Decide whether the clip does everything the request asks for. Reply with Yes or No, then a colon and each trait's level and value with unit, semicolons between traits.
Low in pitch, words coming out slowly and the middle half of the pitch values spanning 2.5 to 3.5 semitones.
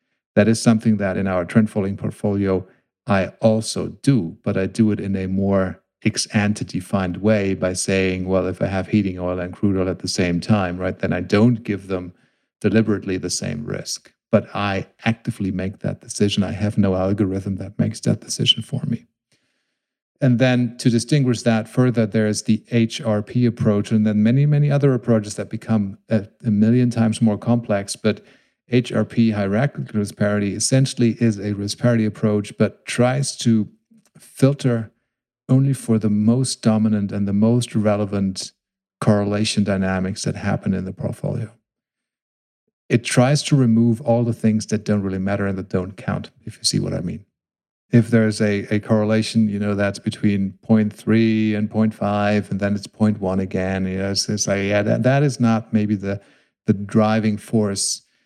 No: low, 105 Hz; average, 175 wpm; average, 2.8 semitones